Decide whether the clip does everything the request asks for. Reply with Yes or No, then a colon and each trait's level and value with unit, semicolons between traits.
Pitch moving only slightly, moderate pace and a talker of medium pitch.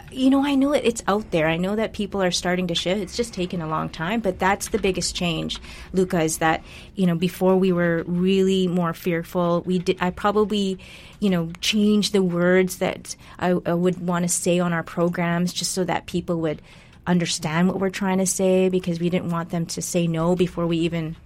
No: narrow, 1.9 semitones; fast, 225 wpm; medium, 180 Hz